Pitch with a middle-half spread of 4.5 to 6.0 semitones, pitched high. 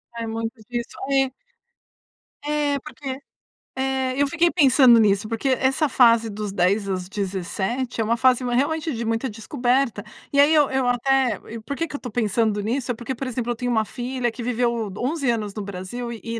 No: average, 3.2 semitones; high, 240 Hz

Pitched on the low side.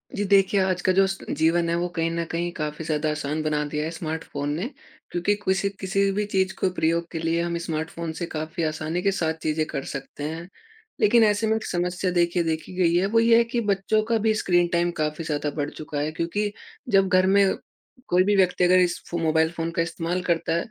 No: medium, 175 Hz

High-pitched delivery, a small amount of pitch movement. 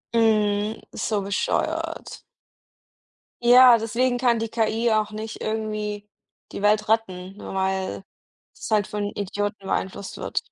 Yes: high, 215 Hz; narrow, 1.7 semitones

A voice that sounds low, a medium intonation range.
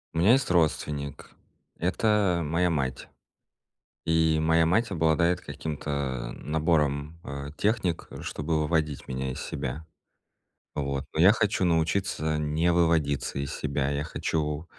Yes: very low, 80 Hz; average, 3.0 semitones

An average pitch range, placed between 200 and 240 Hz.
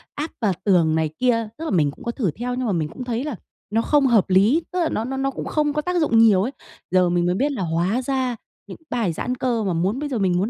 No: wide, 6.3 semitones; high, 230 Hz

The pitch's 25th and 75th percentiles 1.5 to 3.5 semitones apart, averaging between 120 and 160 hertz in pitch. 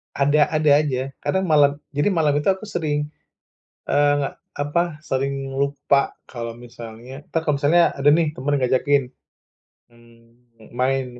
Yes: average, 2.7 semitones; medium, 140 Hz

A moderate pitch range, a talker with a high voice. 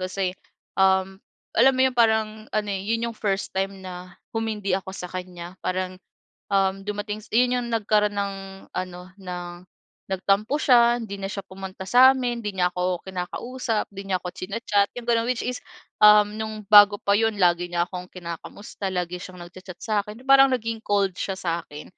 Yes: average, 3.2 semitones; high, 200 Hz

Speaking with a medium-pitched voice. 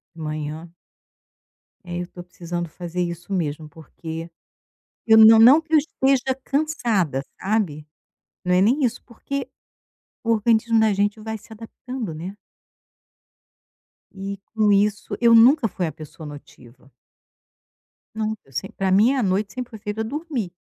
No: high, 205 Hz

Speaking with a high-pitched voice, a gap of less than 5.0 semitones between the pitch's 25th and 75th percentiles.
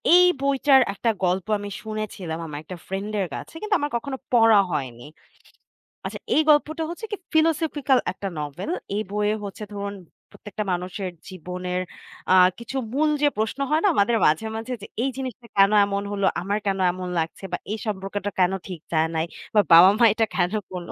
No: high, 205 Hz; wide, 5.6 semitones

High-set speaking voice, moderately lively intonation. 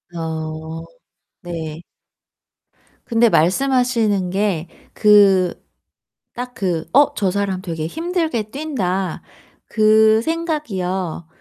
No: high, 200 Hz; wide, 5.9 semitones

